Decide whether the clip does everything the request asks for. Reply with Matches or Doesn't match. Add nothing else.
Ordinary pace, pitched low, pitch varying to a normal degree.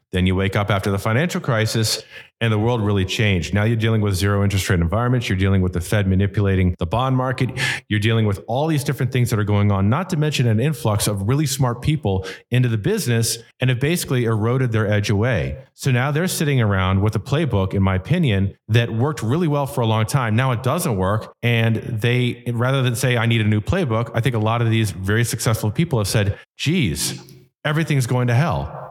Doesn't match